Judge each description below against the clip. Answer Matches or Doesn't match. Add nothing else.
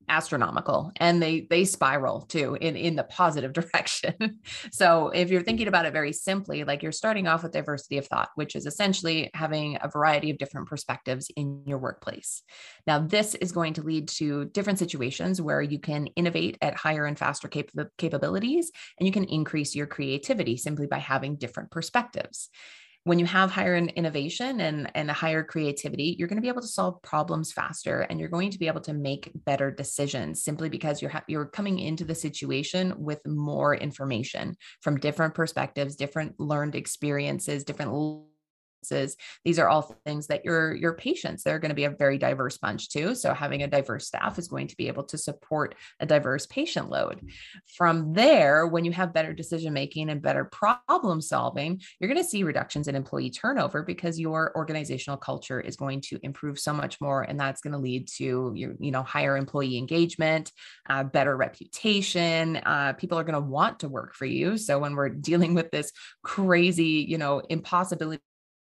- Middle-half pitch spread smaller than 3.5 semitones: Matches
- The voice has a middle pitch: Matches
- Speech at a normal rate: Matches